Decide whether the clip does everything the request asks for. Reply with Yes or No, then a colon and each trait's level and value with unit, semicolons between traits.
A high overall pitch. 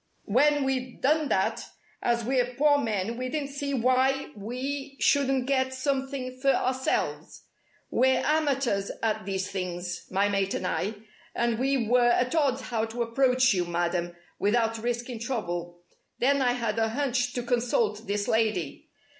Yes: high, 245 Hz